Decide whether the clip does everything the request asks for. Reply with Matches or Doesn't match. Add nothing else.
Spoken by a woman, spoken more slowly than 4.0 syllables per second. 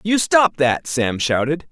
Doesn't match